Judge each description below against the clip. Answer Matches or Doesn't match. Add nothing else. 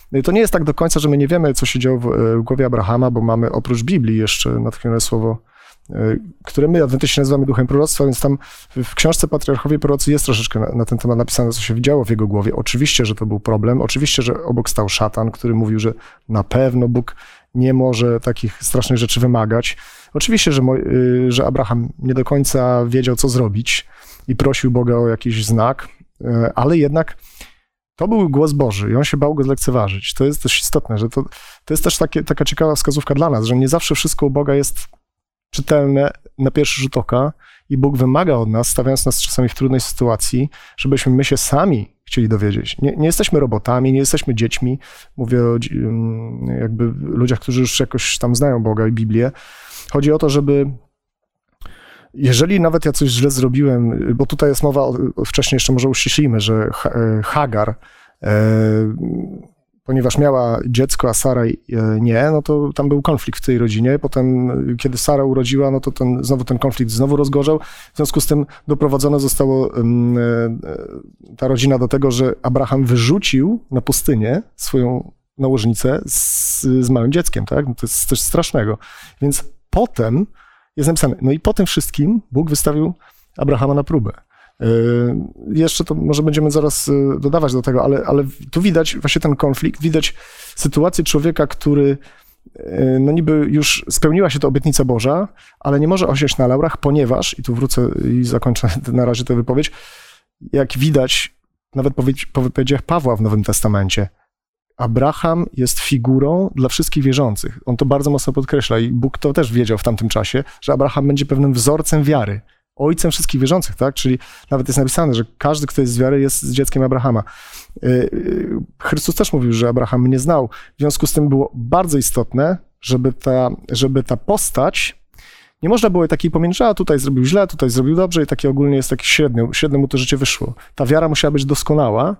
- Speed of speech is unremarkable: Doesn't match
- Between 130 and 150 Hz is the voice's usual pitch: Matches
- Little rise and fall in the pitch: Doesn't match